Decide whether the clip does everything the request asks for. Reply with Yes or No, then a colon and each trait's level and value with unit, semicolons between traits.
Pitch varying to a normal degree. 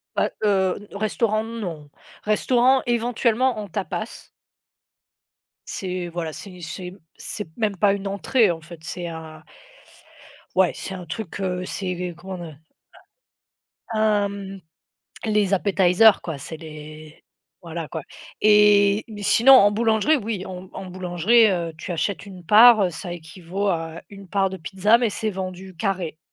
Yes: average, 3.4 semitones